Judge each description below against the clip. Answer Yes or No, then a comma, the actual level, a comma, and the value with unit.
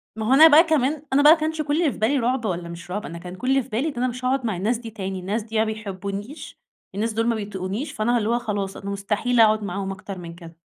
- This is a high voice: Yes, high, 220 Hz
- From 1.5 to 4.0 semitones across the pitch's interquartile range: No, average, 4.6 semitones